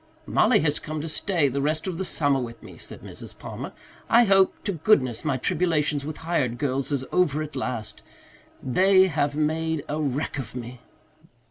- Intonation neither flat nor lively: Yes, average, 3.6 semitones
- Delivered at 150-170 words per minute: No, average, 185 wpm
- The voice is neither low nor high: Yes, medium, 150 Hz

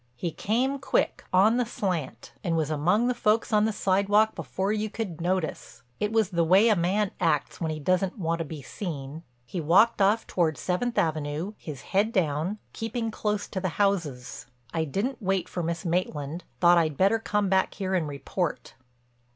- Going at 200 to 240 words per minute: No, average, 185 wpm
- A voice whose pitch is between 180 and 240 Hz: Yes, medium, 185 Hz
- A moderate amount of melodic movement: Yes, average, 4.6 semitones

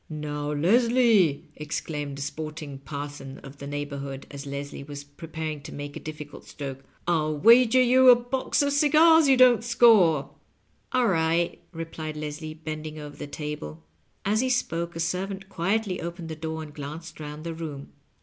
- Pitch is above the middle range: No, medium, 155 Hz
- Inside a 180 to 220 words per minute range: No, average, 170 wpm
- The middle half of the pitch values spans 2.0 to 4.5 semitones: No, average, 5.2 semitones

